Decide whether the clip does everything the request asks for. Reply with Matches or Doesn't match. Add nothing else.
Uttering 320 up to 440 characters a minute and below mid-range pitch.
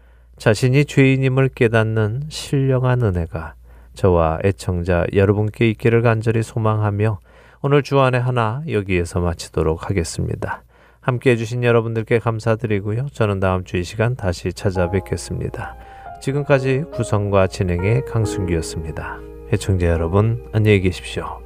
Matches